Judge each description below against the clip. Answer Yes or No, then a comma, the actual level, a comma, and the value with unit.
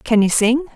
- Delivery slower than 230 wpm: No, fast, 240 wpm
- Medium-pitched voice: No, high, 245 Hz